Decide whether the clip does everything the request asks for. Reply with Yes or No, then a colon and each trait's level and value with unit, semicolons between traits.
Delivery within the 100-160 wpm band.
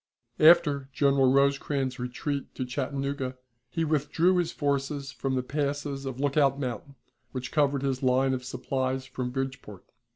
Yes: average, 140 wpm